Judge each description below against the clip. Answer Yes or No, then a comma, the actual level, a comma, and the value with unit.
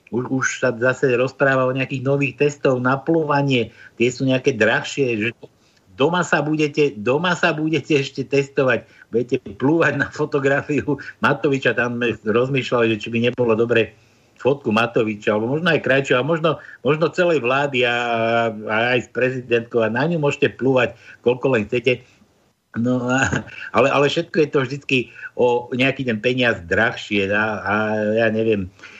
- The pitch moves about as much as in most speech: Yes, average, 3.6 semitones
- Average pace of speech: Yes, average, 155 wpm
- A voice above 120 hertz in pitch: Yes, low, 130 Hz